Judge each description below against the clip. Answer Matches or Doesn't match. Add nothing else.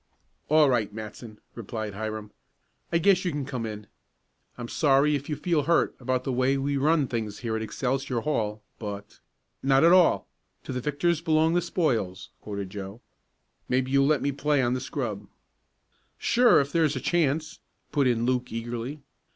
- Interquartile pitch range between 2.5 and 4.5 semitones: Doesn't match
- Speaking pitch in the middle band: Doesn't match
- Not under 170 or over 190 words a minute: Matches